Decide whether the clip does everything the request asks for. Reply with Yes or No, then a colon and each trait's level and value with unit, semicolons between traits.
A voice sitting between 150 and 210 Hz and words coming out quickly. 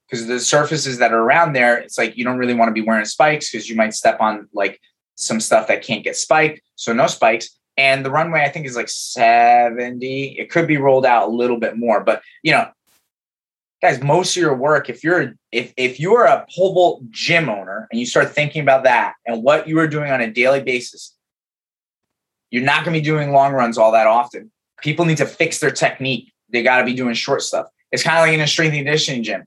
No: low, 135 Hz; fast, 235 wpm